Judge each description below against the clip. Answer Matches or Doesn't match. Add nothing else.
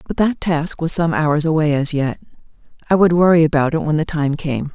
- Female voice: Matches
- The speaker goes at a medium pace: Doesn't match